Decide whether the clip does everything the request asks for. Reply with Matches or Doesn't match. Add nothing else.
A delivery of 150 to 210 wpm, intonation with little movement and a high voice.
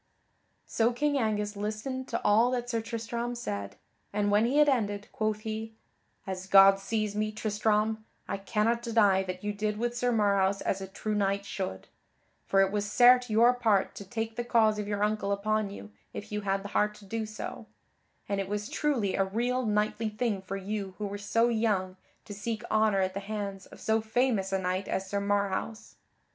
Matches